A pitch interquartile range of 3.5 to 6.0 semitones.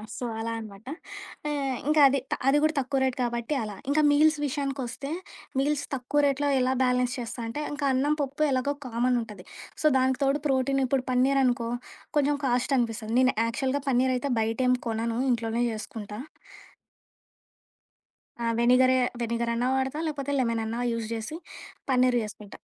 No: average, 3.0 semitones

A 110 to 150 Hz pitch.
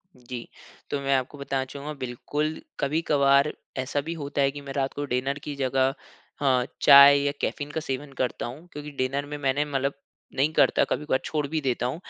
Yes: medium, 140 Hz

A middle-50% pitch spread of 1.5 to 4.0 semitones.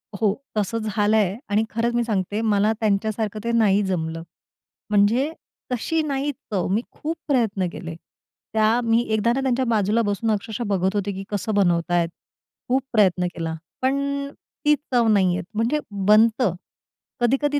Yes: average, 3.1 semitones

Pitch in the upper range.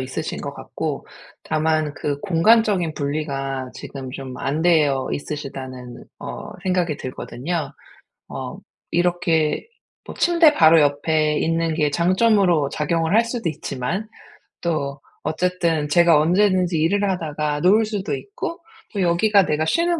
No: medium, 160 Hz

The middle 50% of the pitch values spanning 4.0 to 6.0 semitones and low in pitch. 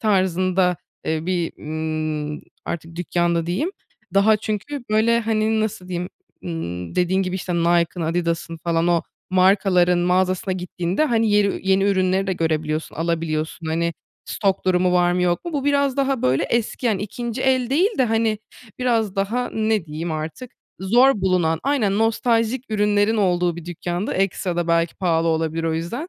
No: average, 4.5 semitones; medium, 185 Hz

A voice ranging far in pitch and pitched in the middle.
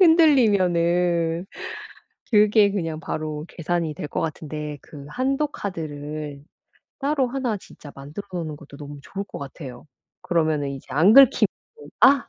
Yes: wide, 5.8 semitones; medium, 170 Hz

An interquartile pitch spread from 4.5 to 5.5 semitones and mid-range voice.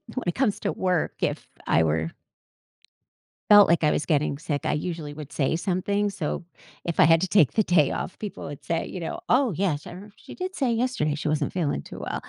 Yes: average, 5.2 semitones; medium, 170 Hz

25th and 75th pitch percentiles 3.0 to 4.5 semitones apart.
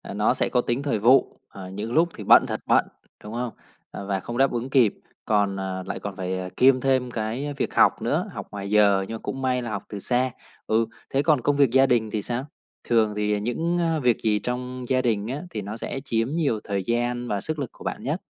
Yes: average, 3.7 semitones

